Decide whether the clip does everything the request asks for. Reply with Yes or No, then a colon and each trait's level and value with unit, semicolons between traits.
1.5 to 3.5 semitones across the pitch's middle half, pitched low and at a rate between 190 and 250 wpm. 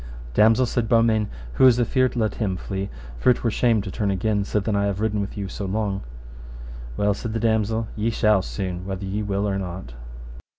Yes: narrow, 2.5 semitones; low, 105 Hz; fast, 205 wpm